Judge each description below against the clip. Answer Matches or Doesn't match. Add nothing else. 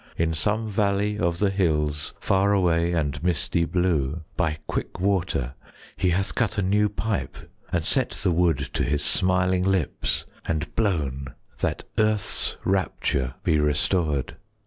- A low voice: Matches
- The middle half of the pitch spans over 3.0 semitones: Matches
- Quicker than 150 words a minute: Doesn't match